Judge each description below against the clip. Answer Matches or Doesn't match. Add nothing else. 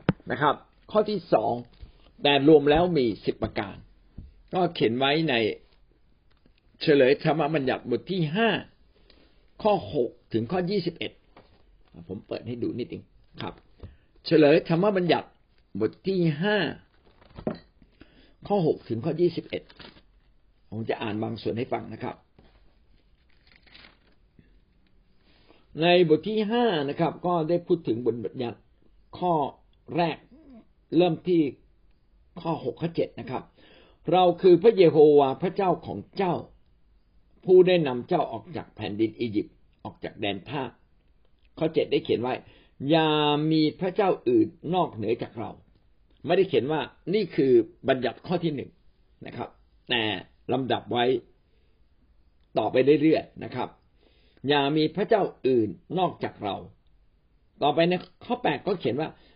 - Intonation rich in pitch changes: Matches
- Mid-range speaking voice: Matches